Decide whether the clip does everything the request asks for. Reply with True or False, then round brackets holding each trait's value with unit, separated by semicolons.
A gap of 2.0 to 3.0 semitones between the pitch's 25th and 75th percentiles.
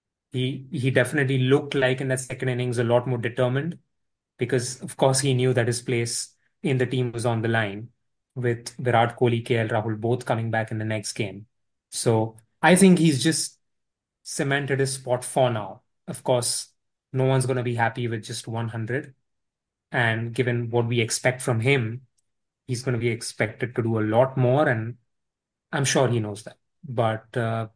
True (2.4 semitones)